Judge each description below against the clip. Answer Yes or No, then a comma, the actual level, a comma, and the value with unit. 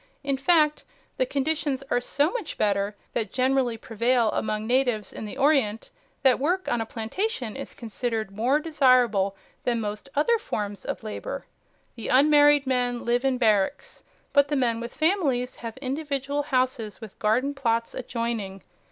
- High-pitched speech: Yes, very high, 250 Hz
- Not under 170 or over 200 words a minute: No, average, 155 wpm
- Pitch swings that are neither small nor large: Yes, average, 4.1 semitones